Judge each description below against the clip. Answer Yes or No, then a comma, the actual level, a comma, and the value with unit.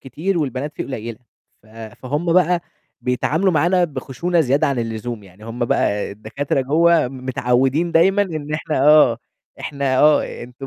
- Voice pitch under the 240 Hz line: Yes, medium, 140 Hz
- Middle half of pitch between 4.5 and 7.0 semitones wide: Yes, average, 5.0 semitones